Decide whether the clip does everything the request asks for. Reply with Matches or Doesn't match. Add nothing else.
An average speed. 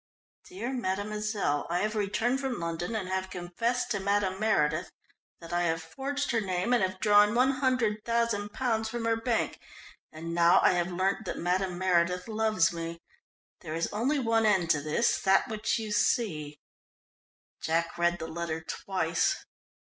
Matches